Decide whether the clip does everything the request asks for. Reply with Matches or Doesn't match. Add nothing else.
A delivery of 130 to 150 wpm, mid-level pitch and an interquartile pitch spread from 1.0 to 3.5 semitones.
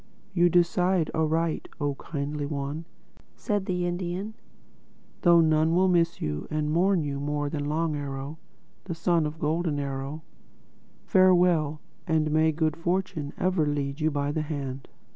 Matches